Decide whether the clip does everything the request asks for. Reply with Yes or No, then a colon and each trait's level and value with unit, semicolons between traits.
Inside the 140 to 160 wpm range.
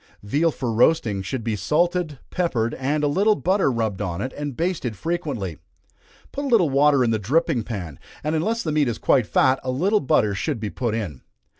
No: average, 200 wpm